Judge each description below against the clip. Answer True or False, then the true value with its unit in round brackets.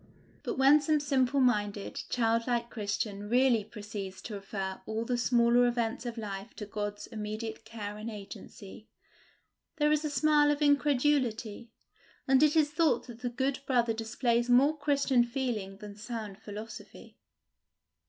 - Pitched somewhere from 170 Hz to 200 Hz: False (235 Hz)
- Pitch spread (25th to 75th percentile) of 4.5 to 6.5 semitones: False (4.1 semitones)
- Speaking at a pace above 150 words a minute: False (145 wpm)